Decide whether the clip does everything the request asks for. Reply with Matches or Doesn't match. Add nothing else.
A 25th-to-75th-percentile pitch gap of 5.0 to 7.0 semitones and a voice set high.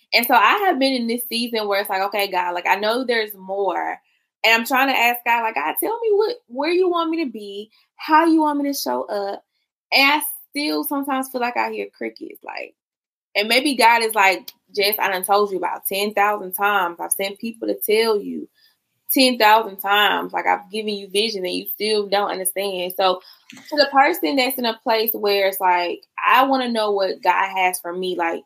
Matches